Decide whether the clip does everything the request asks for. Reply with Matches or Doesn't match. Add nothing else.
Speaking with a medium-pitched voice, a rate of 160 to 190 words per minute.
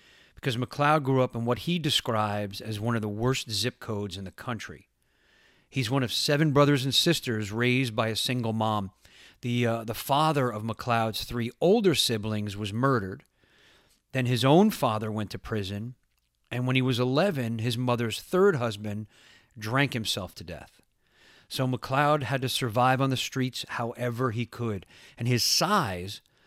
Doesn't match